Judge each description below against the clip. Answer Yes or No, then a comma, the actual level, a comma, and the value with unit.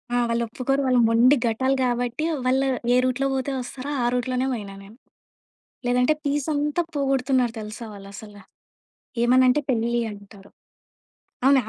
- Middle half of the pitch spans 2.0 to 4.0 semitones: Yes, average, 2.8 semitones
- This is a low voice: No, very high, 250 Hz